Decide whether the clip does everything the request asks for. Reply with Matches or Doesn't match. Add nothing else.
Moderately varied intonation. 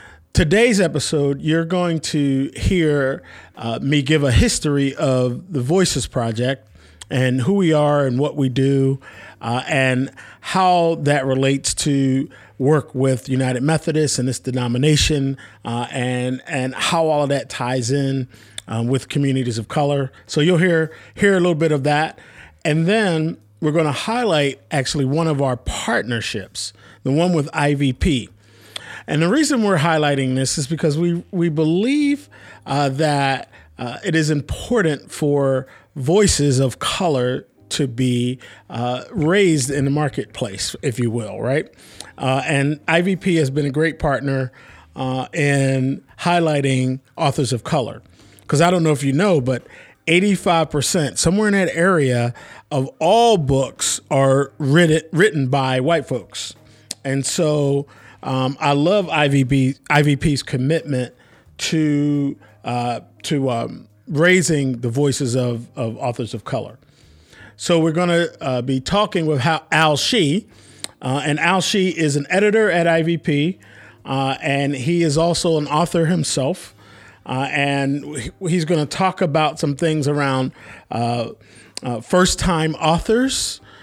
Matches